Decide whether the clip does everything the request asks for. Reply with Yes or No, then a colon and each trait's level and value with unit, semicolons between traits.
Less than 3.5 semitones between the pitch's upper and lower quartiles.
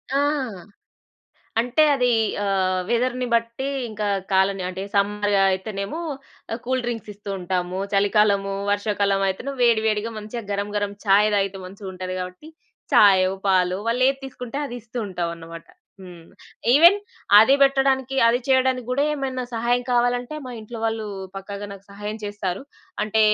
No: average, 3.9 semitones